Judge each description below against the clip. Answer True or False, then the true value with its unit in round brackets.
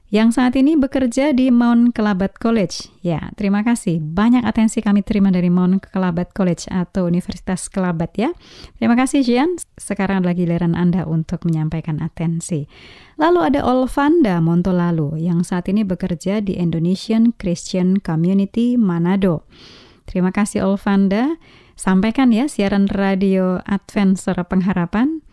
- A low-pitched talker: False (195 Hz)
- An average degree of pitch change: True (4.5 semitones)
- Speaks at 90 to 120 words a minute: False (135 wpm)